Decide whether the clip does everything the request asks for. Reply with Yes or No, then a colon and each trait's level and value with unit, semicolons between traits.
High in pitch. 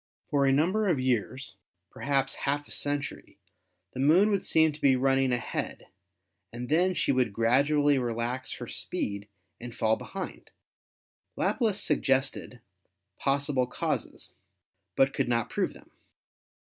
No: low, 135 Hz